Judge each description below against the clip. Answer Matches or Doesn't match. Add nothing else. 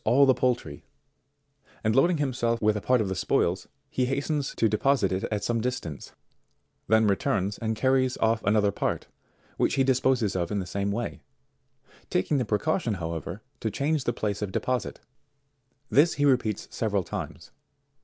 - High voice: Doesn't match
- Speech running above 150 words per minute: Matches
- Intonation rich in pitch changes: Doesn't match